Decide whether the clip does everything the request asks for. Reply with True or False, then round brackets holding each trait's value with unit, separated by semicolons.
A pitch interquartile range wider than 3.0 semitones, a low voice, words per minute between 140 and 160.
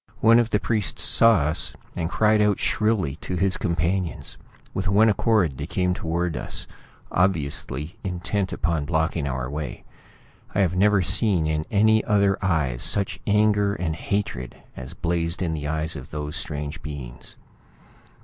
True (4.9 semitones; 85 Hz; 155 wpm)